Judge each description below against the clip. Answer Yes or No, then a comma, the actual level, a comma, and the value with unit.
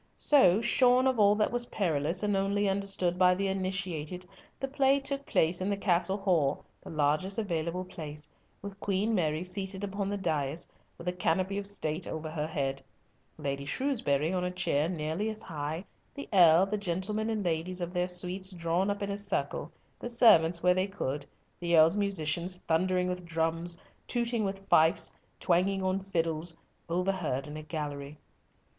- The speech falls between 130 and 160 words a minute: No, average, 175 wpm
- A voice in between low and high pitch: Yes, medium, 180 Hz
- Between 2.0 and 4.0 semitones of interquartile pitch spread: Yes, average, 3.6 semitones